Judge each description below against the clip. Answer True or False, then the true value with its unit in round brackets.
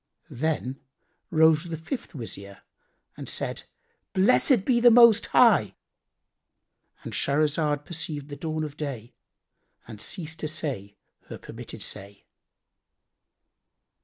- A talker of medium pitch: True (155 Hz)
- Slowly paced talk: True (105 wpm)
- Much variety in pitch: False (3.5 semitones)